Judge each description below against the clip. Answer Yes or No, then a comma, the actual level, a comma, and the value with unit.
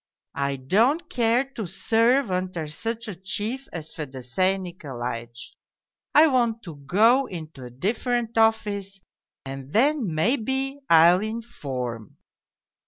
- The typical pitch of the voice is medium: No, high, 195 Hz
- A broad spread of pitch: Yes, wide, 7.5 semitones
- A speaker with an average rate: No, slow, 115 wpm